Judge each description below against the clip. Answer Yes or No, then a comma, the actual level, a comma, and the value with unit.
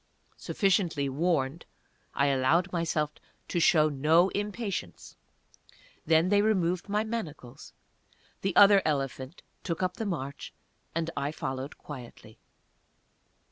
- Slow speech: Yes, slow, 110 wpm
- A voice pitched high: No, medium, 165 Hz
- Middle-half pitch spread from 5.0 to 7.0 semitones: Yes, average, 5.3 semitones